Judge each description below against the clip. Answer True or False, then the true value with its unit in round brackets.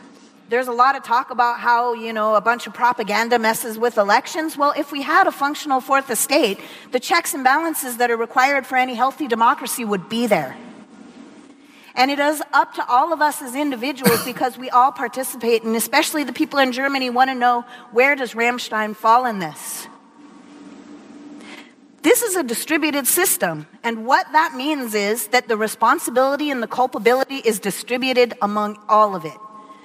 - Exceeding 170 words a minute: True (180 wpm)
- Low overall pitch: False (250 Hz)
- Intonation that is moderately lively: True (3.5 semitones)